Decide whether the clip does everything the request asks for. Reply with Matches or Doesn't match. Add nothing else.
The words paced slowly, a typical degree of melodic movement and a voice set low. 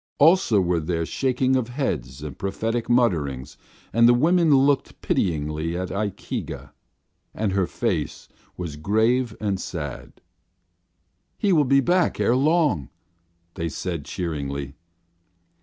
Doesn't match